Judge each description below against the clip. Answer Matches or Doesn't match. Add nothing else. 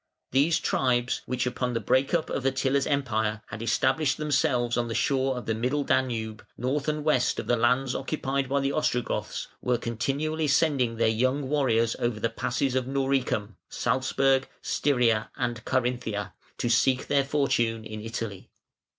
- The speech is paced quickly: Doesn't match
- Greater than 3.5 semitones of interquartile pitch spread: Doesn't match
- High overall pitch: Doesn't match